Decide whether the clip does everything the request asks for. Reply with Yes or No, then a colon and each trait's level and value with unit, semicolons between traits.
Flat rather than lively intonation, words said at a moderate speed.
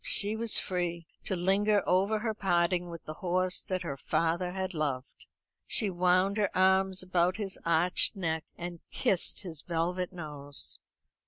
Yes: narrow, 2.1 semitones; average, 155 wpm